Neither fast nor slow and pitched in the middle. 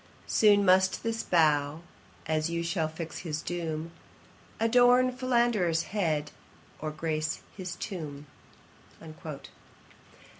No: slow, 100 wpm; medium, 170 Hz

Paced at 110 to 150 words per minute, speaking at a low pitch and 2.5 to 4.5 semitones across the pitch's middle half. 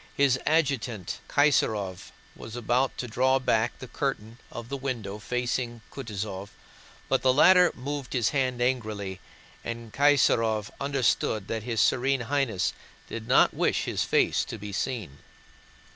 Yes: average, 140 wpm; low, 120 Hz; average, 3.6 semitones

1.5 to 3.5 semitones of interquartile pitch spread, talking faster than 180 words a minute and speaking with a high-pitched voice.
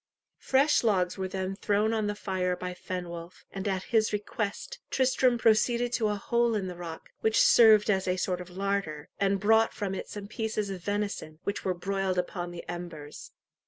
Yes: average, 3.1 semitones; average, 190 wpm; high, 195 Hz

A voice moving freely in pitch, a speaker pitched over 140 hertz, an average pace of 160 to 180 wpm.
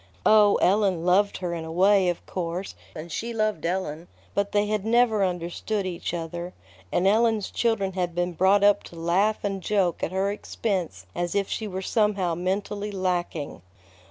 No: average, 3.0 semitones; high, 190 Hz; average, 175 wpm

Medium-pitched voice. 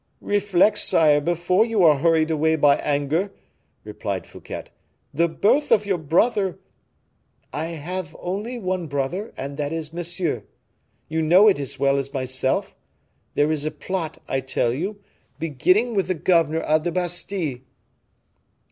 Yes: medium, 165 Hz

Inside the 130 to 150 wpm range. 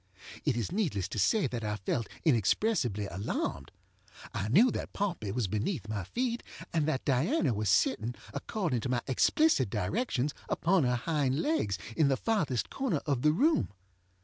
No: average, 165 wpm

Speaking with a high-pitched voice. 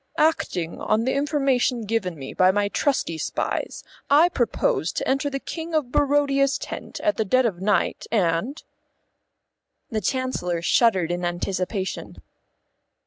Yes: high, 230 Hz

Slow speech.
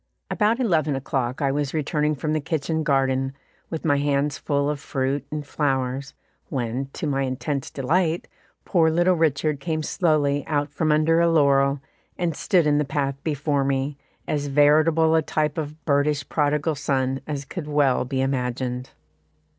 No: average, 165 wpm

